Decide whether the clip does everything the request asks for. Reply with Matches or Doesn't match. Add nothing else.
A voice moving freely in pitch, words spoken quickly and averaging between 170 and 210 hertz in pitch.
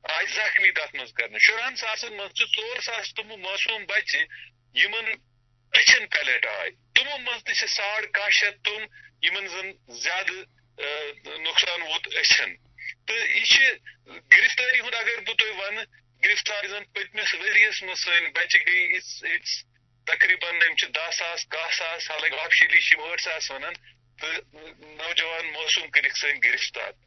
Doesn't match